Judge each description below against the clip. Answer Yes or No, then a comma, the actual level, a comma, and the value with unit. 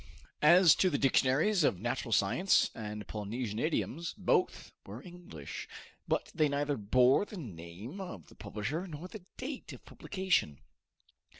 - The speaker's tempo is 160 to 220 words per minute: No, average, 140 wpm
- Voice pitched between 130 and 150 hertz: Yes, medium, 140 Hz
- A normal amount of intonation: No, wide, 8.8 semitones